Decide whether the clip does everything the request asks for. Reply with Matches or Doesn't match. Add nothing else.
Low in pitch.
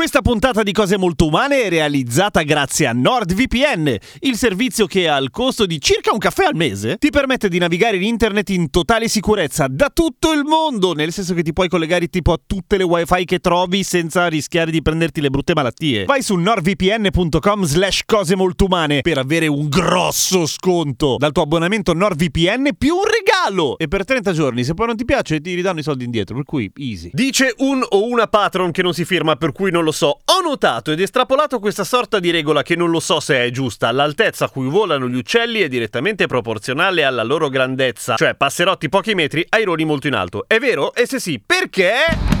Doesn't match